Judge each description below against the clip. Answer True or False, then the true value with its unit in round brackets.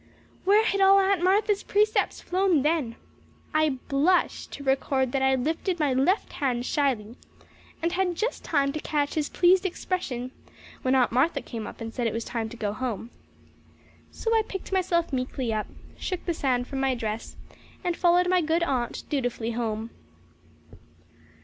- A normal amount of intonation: False (6.6 semitones)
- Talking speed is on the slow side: False (170 wpm)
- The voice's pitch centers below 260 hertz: False (285 Hz)